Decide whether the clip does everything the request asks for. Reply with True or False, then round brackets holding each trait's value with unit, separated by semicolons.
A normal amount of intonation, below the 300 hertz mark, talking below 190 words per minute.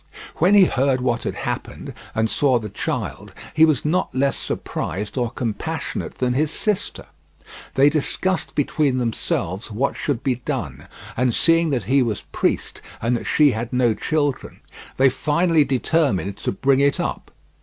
True (4.1 semitones; 135 Hz; 160 wpm)